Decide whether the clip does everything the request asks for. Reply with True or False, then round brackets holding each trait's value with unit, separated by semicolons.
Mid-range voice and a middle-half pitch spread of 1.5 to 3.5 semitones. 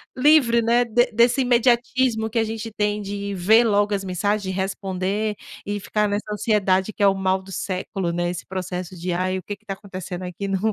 False (205 Hz; 2.8 semitones)